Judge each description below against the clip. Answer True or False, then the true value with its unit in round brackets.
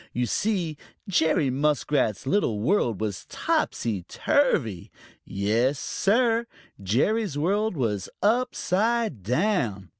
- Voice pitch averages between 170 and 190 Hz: False (150 Hz)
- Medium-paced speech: False (95 wpm)